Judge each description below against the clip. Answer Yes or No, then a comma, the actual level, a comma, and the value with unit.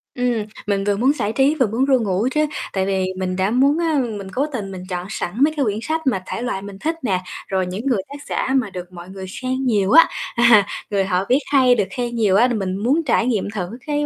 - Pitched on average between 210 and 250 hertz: Yes, high, 220 Hz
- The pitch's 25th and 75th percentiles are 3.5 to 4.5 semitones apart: No, average, 5.2 semitones